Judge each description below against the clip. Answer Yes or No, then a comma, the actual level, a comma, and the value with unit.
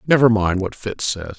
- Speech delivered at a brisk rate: Yes, fast, 215 wpm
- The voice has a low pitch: Yes, low, 105 Hz